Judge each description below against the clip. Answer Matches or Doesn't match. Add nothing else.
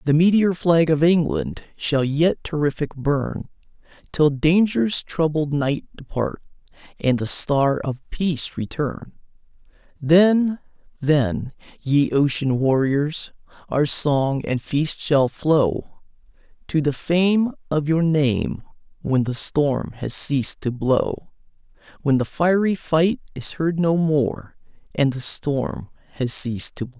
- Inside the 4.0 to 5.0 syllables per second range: Doesn't match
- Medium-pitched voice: Matches